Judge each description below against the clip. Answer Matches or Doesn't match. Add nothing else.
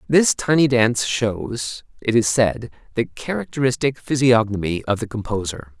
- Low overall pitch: Matches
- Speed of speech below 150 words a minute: Matches